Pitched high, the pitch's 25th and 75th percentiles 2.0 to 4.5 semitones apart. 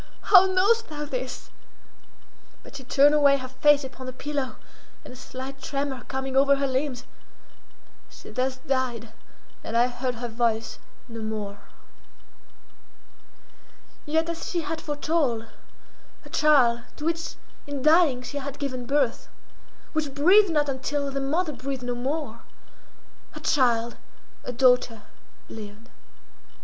Yes: very high, 270 Hz; average, 3.2 semitones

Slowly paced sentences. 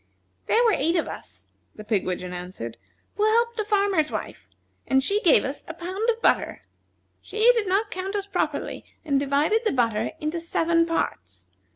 No: average, 175 wpm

